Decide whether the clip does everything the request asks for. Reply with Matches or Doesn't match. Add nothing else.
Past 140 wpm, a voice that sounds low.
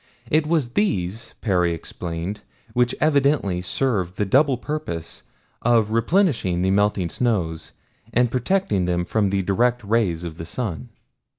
Doesn't match